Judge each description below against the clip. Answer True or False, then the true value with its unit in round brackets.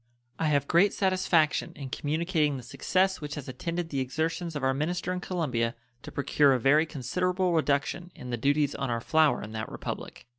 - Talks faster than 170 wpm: True (190 wpm)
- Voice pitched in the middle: True (150 Hz)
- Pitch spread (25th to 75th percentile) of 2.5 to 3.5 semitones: False (4.2 semitones)